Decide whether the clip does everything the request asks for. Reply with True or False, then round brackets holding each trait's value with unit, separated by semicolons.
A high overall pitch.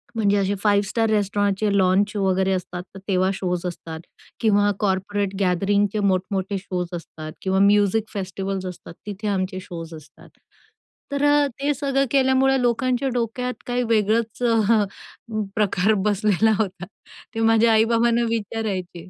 True (205 Hz)